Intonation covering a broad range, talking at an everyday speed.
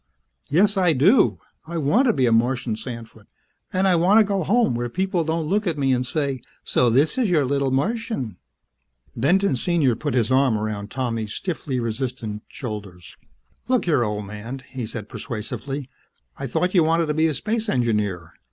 Yes: wide, 6.8 semitones; average, 180 wpm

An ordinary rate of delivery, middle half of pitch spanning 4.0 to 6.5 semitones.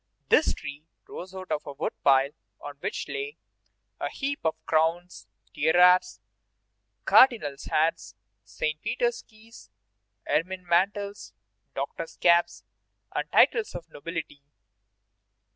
No: slow, 110 wpm; average, 4.7 semitones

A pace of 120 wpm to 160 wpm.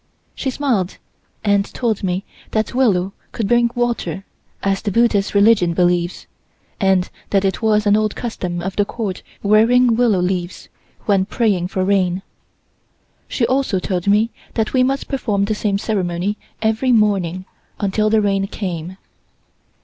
Yes: average, 150 wpm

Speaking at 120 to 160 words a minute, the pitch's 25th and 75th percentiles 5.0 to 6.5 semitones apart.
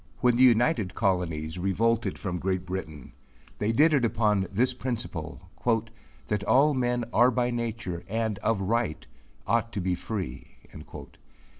No: average, 140 wpm; average, 4.5 semitones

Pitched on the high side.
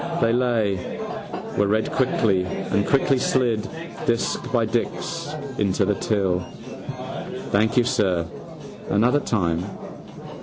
No: low, 105 Hz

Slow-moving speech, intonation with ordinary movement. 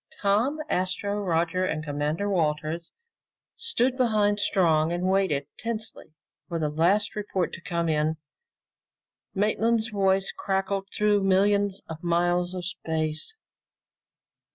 Yes: slow, 115 wpm; average, 3.8 semitones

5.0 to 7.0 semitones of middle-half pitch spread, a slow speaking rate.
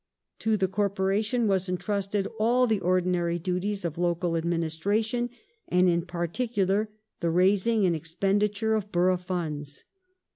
No: average, 3.3 semitones; slow, 125 wpm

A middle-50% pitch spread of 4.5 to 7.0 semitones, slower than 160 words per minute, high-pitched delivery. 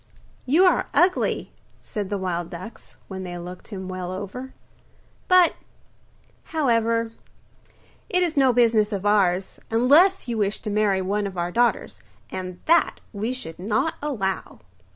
Yes: average, 5.2 semitones; average, 150 wpm; high, 210 Hz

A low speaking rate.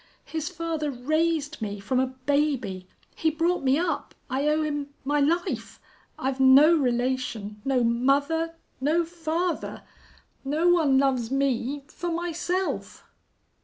Yes: slow, 130 wpm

